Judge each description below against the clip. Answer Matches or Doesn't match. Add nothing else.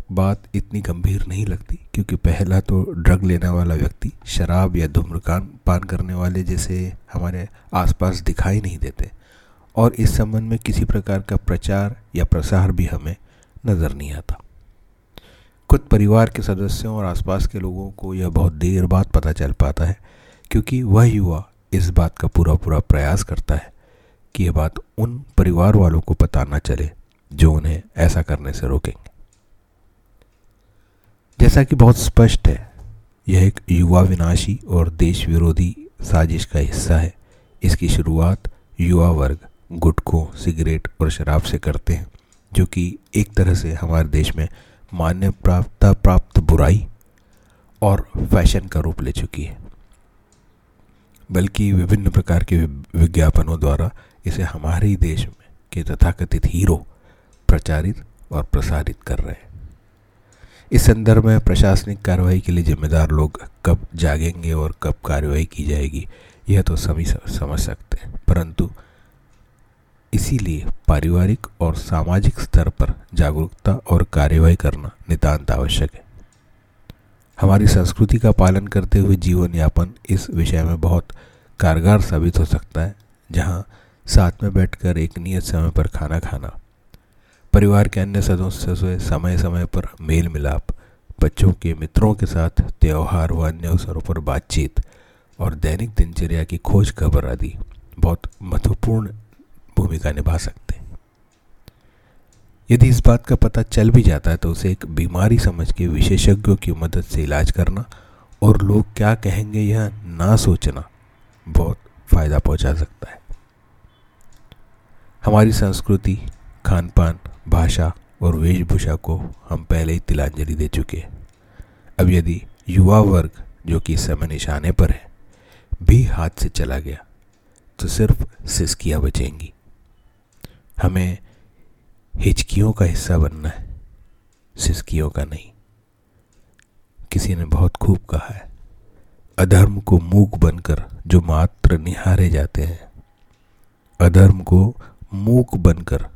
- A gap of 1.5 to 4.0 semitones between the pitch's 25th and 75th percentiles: Matches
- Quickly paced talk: Doesn't match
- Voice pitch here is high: Doesn't match